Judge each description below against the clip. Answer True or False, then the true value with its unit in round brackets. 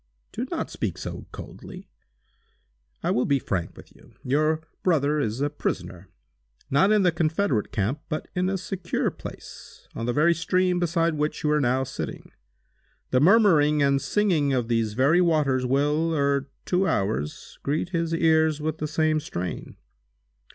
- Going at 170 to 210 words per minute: False (160 wpm)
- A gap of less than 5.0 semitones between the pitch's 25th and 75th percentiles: True (4.1 semitones)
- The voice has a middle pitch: True (150 Hz)